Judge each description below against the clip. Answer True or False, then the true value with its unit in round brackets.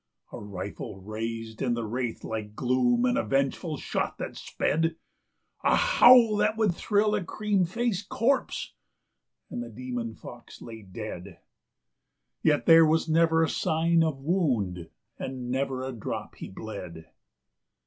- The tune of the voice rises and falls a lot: True (8.2 semitones)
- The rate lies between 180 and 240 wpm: False (145 wpm)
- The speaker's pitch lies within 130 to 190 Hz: True (135 Hz)